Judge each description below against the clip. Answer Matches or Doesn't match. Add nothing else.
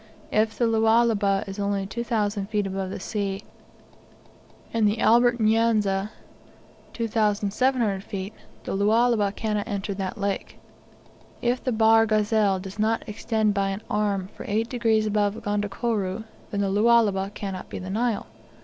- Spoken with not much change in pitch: Matches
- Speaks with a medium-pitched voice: Doesn't match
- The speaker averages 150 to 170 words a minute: Doesn't match